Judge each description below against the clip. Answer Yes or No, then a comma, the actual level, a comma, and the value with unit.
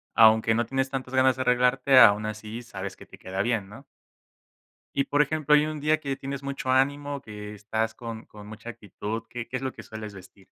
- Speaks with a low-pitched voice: Yes, low, 120 Hz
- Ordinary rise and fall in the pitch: Yes, average, 4.0 semitones